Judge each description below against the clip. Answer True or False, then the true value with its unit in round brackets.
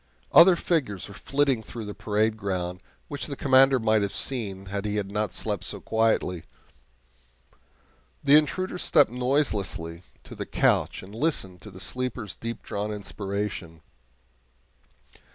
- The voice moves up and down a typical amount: True (5.0 semitones)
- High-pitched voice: False (105 Hz)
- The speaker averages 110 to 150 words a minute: True (135 wpm)